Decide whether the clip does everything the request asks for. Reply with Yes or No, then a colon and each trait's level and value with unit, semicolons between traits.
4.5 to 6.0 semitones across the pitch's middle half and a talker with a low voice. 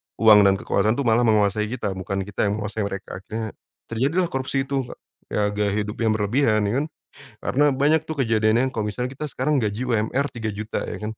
No: average, 4.0 semitones; low, 110 Hz